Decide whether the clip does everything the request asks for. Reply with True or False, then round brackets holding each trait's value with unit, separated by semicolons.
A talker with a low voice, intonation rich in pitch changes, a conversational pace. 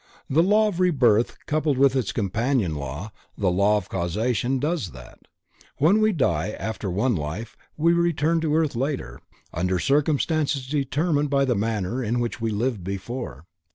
True (125 Hz; 7.1 semitones; 160 wpm)